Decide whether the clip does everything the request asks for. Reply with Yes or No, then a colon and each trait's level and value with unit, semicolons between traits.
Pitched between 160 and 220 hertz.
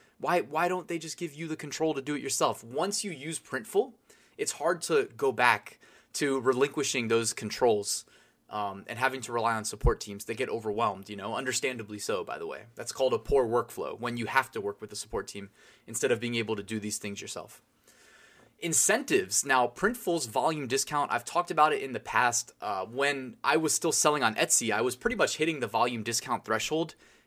No: low, 135 Hz